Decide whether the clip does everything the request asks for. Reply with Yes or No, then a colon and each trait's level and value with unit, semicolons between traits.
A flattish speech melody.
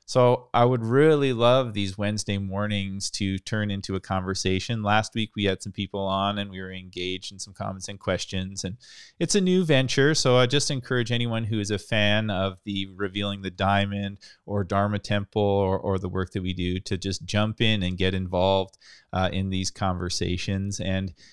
Yes: narrow, 2.2 semitones